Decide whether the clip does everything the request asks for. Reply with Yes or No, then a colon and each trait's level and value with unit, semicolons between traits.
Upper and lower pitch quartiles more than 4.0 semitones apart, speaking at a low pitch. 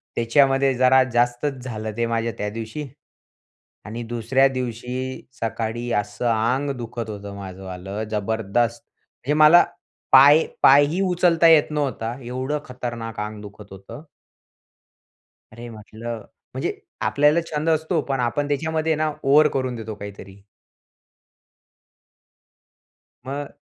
Yes: average, 4.5 semitones; low, 120 Hz